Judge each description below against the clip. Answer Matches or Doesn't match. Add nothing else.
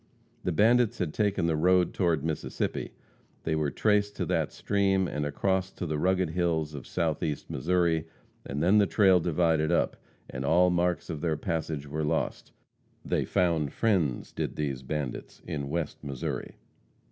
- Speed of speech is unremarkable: Matches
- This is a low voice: Matches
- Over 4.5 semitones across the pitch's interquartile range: Doesn't match